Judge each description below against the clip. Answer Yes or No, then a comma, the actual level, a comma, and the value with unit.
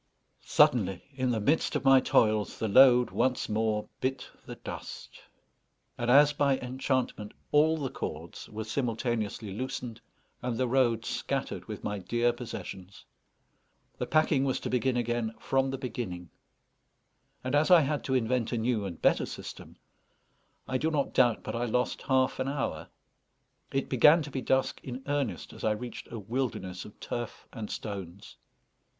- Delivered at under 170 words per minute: Yes, average, 160 wpm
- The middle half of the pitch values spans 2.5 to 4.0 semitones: Yes, average, 3.4 semitones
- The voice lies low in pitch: Yes, low, 125 Hz